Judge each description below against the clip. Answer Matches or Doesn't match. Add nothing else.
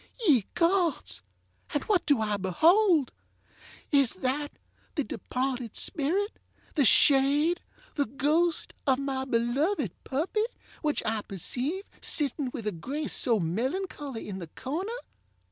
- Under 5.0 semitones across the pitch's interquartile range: Doesn't match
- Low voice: Doesn't match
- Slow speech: Matches